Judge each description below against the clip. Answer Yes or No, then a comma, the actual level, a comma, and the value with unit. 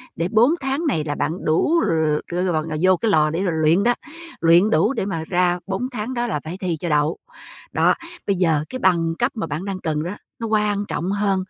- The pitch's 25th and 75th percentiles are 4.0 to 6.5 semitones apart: Yes, average, 4.7 semitones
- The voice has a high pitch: No, medium, 180 Hz